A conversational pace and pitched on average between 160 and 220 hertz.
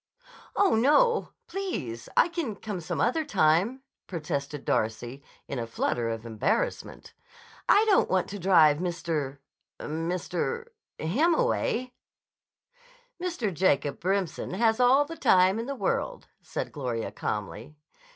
No: slow, 120 wpm; medium, 185 Hz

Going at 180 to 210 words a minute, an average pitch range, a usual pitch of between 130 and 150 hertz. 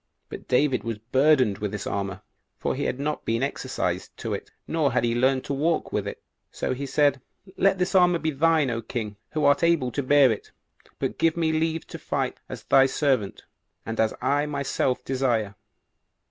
Yes: average, 195 wpm; average, 4.6 semitones; low, 135 Hz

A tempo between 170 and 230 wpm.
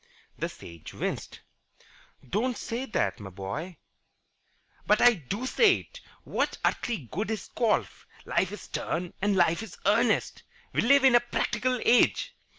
No: average, 150 wpm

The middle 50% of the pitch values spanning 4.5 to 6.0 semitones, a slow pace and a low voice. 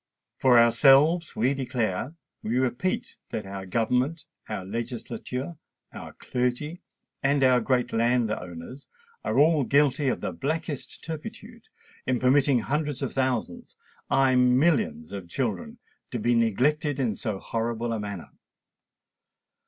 No: average, 4.0 semitones; slow, 120 wpm; low, 125 Hz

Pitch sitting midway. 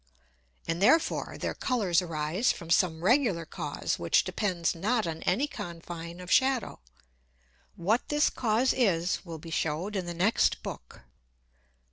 Yes: medium, 180 Hz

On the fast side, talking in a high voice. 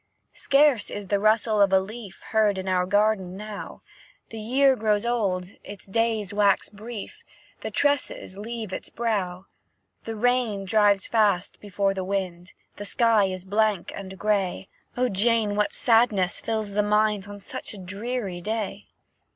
No: average, 155 wpm; high, 205 Hz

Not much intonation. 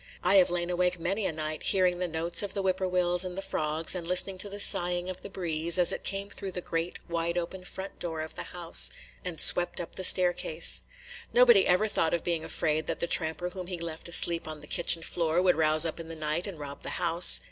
Yes: narrow, 1.9 semitones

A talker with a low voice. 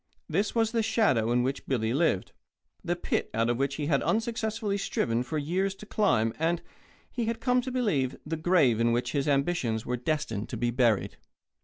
No: medium, 150 Hz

